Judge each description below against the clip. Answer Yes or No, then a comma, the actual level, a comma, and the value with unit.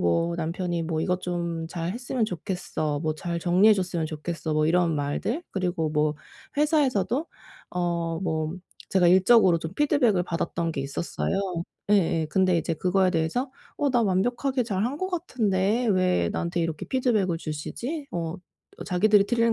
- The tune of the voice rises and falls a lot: No, average, 4.7 semitones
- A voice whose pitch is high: No, medium, 180 Hz